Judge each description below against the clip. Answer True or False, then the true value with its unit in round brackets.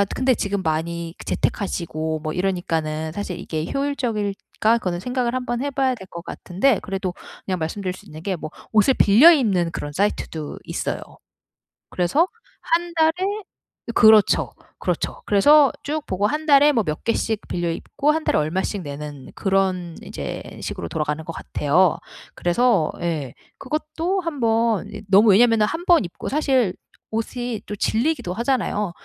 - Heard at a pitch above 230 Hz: False (205 Hz)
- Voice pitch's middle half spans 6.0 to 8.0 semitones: True (7.1 semitones)